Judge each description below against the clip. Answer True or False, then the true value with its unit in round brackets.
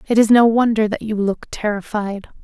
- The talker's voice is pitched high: True (215 Hz)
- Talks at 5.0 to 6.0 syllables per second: True (5.2 syllables/s)